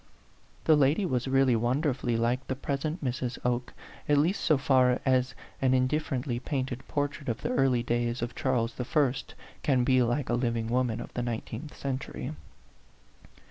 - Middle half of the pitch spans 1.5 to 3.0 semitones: Yes, narrow, 2.4 semitones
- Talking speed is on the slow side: No, average, 165 wpm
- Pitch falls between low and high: No, low, 130 Hz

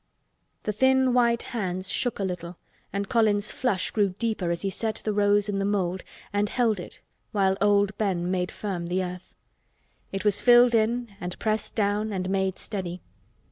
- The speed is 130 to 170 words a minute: No, average, 180 wpm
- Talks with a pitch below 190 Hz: No, high, 205 Hz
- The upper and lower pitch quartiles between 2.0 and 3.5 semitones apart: Yes, average, 2.7 semitones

